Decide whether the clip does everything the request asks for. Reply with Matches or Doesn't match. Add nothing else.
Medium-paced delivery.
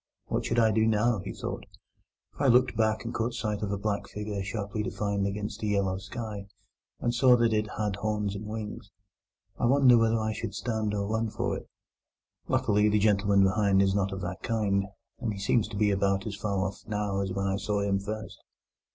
Doesn't match